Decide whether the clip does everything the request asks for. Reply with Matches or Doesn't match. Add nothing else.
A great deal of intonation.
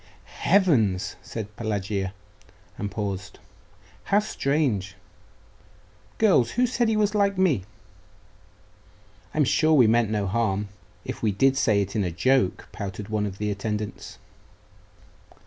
Matches